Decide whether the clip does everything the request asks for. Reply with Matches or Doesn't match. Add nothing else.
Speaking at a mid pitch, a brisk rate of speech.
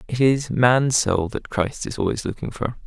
Doesn't match